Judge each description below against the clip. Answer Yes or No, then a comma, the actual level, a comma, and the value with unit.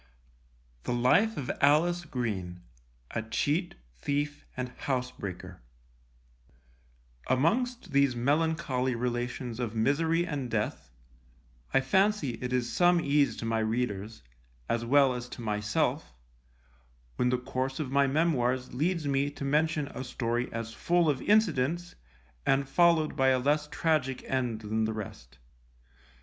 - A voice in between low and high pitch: No, low, 130 Hz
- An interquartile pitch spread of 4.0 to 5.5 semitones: Yes, average, 4.3 semitones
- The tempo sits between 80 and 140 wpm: Yes, slow, 135 wpm